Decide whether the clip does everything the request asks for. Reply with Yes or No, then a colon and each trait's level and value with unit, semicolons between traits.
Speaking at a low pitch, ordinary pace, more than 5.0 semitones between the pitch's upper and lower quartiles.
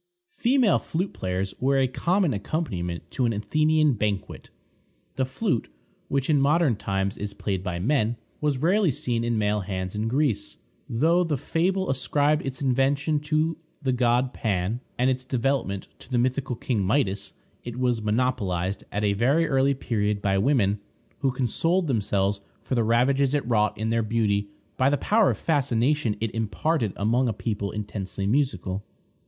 Yes: low, 125 Hz; average, 165 wpm; wide, 5.5 semitones